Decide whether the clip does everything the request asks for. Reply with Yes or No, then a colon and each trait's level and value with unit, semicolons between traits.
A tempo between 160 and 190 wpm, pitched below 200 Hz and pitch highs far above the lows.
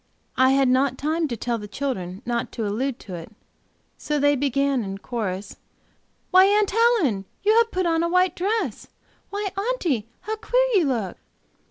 No: average, 175 wpm; very high, 280 Hz; wide, 8.3 semitones